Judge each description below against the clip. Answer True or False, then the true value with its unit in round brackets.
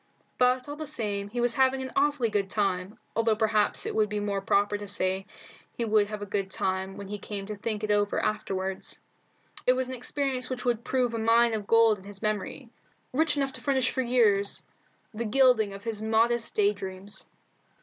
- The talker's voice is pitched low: False (215 Hz)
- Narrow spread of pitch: False (3.4 semitones)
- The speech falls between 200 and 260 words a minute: True (205 wpm)